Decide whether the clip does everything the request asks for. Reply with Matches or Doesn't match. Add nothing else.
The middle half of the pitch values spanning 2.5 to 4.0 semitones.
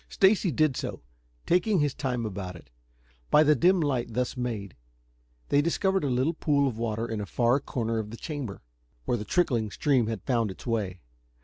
Doesn't match